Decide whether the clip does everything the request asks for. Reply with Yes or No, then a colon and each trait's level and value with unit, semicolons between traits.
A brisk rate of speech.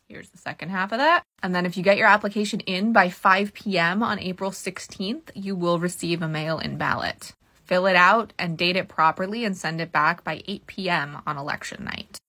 Yes: fast, 215 wpm